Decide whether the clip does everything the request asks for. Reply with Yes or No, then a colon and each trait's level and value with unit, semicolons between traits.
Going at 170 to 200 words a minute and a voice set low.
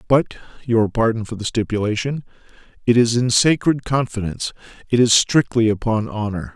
No: average, 145 wpm; low, 115 Hz